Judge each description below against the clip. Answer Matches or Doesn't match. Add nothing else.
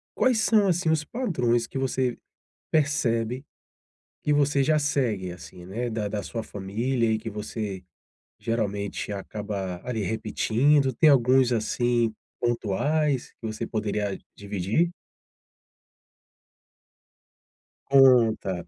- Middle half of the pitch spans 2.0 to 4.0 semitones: Doesn't match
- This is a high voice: Doesn't match